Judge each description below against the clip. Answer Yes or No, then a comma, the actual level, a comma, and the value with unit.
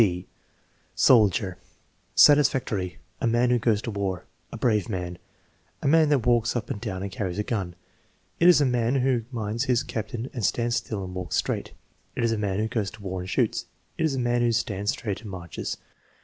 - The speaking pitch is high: No, low, 110 Hz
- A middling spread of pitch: Yes, average, 3.9 semitones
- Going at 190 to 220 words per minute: Yes, fast, 205 wpm